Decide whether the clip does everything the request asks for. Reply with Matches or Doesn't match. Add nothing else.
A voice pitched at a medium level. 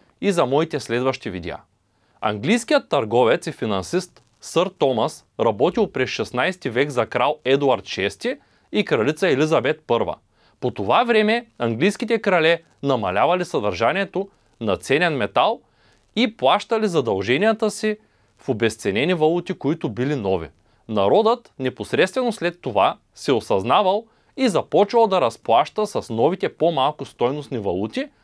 Matches